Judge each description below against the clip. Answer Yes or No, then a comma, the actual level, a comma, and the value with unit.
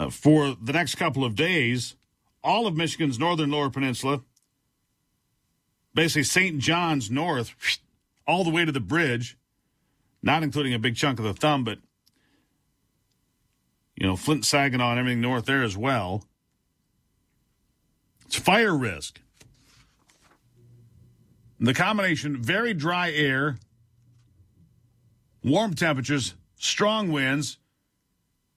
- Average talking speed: No, slow, 115 wpm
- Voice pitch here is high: No, low, 135 Hz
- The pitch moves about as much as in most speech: Yes, average, 4.3 semitones